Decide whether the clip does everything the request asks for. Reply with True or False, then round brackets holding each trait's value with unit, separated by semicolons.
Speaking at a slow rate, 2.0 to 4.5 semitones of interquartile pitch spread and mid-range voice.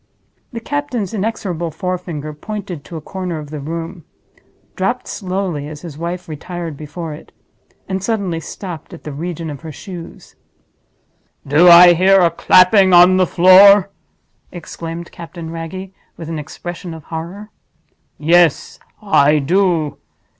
True (130 wpm; 2.8 semitones; 175 Hz)